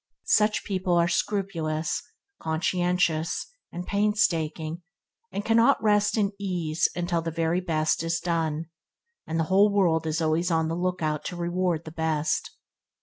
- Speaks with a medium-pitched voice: Yes, medium, 170 Hz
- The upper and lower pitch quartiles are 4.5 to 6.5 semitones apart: No, average, 2.7 semitones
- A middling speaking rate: Yes, average, 145 wpm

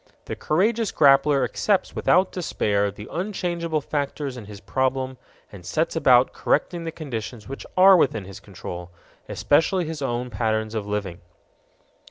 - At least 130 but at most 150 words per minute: Yes, average, 145 wpm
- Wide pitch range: Yes, wide, 7.3 semitones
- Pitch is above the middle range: No, low, 135 Hz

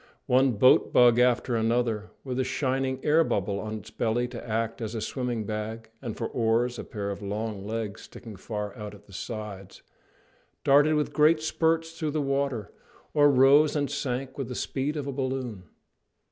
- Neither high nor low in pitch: No, low, 120 Hz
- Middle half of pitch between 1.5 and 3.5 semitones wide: No, average, 4.1 semitones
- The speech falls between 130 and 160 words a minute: No, average, 185 wpm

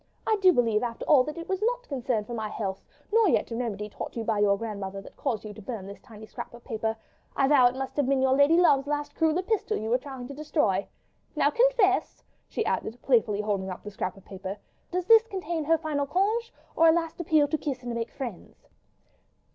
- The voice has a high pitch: Yes, very high, 260 Hz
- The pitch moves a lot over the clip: Yes, wide, 7.1 semitones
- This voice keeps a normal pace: No, fast, 230 wpm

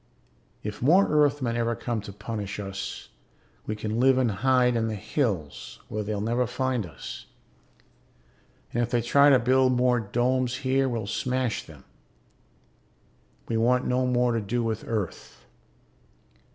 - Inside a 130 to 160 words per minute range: Yes, average, 150 wpm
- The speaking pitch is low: Yes, low, 120 Hz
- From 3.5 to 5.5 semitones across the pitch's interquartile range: No, average, 2.9 semitones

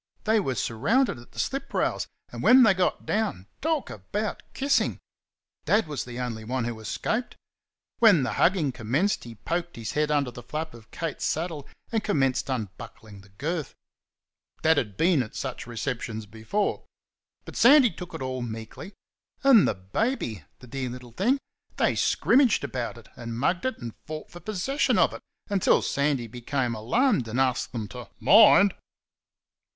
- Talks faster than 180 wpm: No, average, 165 wpm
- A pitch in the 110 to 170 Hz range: Yes, medium, 140 Hz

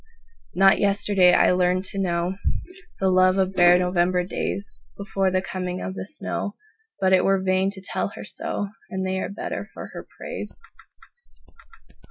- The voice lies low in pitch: No, high, 190 Hz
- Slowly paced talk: No, average, 145 wpm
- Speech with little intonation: Yes, narrow, 1.3 semitones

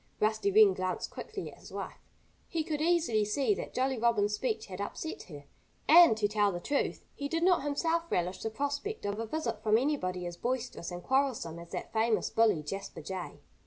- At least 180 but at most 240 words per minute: Yes, average, 200 wpm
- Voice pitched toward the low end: No, high, 220 Hz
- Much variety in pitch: Yes, wide, 6.3 semitones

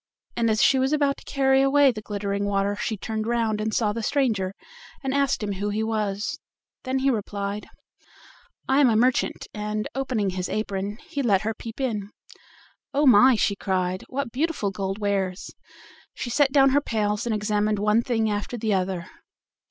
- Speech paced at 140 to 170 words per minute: No, average, 185 wpm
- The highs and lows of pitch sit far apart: No, average, 4.3 semitones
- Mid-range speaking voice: No, high, 215 Hz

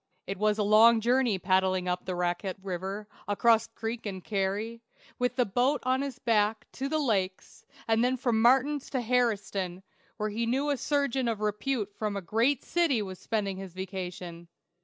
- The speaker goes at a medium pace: Yes, average, 180 wpm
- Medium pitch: No, high, 215 Hz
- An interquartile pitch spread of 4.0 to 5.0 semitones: Yes, average, 4.5 semitones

